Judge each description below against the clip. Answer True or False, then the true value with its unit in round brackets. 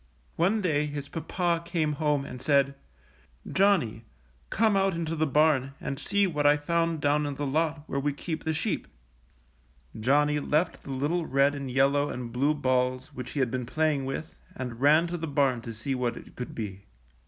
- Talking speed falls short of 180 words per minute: False (195 wpm)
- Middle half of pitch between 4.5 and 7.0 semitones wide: False (3.2 semitones)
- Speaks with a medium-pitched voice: True (145 Hz)